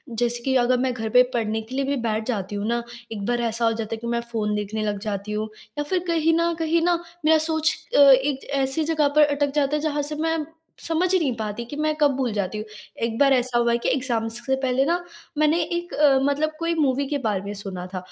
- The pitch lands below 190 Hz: No, very high, 255 Hz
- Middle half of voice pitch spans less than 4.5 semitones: No, average, 5.2 semitones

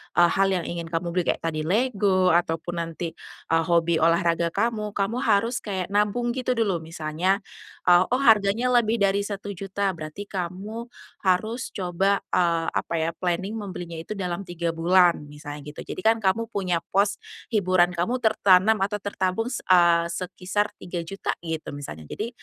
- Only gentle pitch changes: No, average, 3.4 semitones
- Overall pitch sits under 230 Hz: Yes, medium, 185 Hz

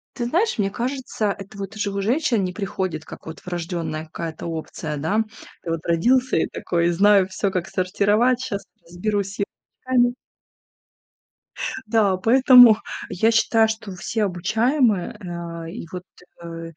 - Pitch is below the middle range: No, high, 200 Hz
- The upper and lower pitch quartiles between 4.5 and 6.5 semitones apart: Yes, average, 4.8 semitones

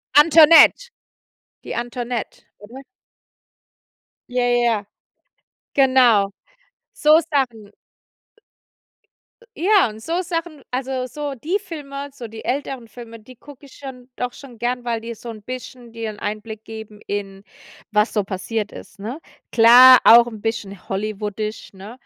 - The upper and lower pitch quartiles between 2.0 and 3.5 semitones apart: No, average, 3.9 semitones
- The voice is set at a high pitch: Yes, high, 240 Hz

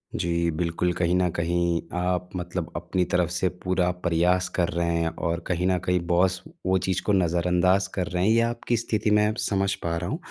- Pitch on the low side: Yes, very low, 90 Hz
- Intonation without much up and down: Yes, narrow, 1.4 semitones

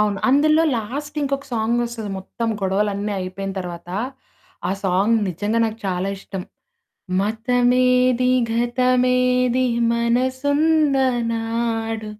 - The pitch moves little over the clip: No, average, 3.3 semitones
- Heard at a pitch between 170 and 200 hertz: No, high, 235 Hz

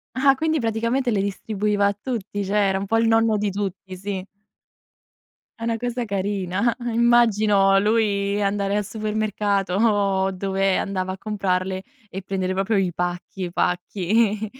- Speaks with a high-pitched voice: Yes, high, 200 Hz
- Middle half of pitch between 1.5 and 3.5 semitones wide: Yes, narrow, 2.5 semitones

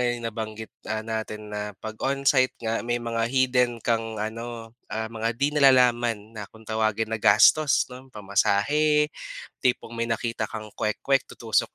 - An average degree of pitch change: No, narrow, 2.3 semitones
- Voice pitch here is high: No, low, 115 Hz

